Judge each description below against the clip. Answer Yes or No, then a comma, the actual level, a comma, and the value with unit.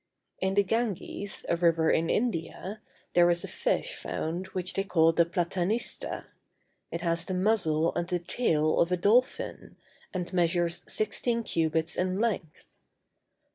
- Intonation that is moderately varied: Yes, average, 3.2 semitones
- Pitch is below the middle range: No, medium, 180 Hz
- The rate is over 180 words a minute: No, average, 145 wpm